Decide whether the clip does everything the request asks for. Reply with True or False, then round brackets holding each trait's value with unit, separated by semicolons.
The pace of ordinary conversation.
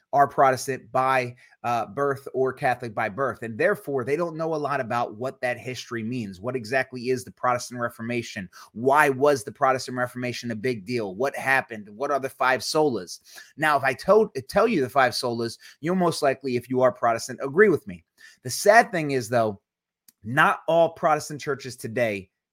True (190 wpm)